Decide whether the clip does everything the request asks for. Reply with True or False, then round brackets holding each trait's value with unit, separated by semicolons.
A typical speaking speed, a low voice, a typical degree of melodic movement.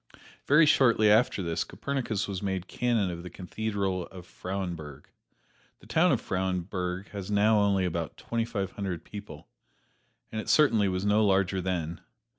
True (155 wpm; 95 Hz; 3.0 semitones)